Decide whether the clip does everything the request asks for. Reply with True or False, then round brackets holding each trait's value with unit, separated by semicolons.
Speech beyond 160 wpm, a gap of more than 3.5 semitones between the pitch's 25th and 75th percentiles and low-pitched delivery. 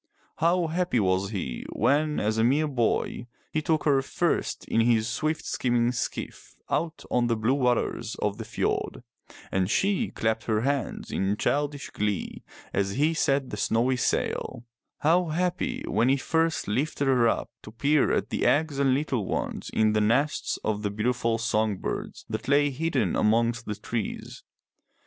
True (170 wpm; 5.1 semitones; 125 Hz)